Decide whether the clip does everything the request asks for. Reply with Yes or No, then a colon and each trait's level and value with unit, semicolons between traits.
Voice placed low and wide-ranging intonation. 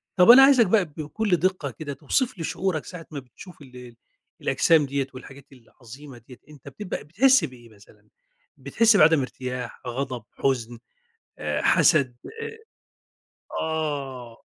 No: medium, 145 Hz; wide, 6.0 semitones